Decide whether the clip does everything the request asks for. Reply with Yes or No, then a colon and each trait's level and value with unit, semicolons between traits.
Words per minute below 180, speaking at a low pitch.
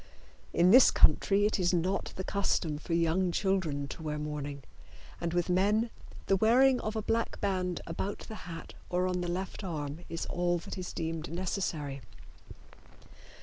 No: average, 165 wpm; medium, 180 Hz